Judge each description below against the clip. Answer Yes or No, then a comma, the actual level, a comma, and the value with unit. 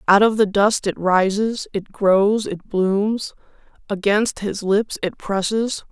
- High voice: Yes, high, 205 Hz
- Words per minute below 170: Yes, average, 150 wpm